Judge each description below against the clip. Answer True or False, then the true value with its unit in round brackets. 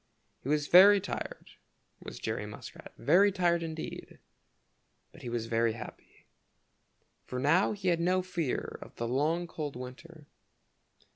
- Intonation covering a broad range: True (5.9 semitones)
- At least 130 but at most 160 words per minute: True (140 wpm)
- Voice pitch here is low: False (165 Hz)